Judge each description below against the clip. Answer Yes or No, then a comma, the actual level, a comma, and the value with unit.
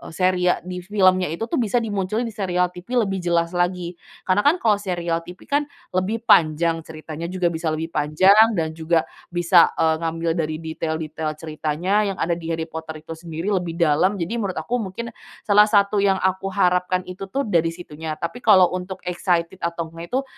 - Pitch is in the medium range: Yes, medium, 180 Hz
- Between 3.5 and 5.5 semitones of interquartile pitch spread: No, average, 3.0 semitones